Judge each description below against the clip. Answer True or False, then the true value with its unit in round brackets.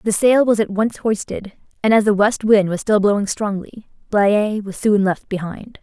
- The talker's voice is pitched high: True (210 Hz)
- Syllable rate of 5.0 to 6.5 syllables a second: False (4.6 syllables/s)